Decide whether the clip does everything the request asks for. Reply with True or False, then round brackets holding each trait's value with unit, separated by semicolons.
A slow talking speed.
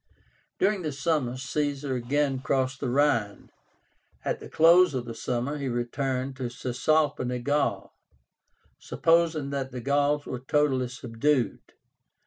True (125 wpm)